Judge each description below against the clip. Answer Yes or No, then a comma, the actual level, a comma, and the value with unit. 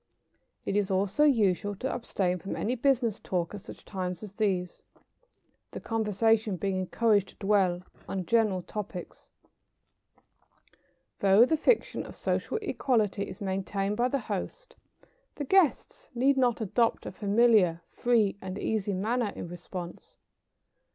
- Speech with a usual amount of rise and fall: Yes, average, 3.8 semitones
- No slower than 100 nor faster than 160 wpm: Yes, average, 140 wpm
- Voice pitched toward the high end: Yes, high, 205 Hz